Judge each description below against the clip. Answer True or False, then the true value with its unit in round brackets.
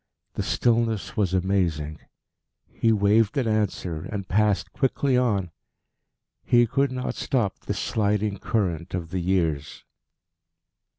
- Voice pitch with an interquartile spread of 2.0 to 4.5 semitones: True (4.0 semitones)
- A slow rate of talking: True (120 wpm)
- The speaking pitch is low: True (100 Hz)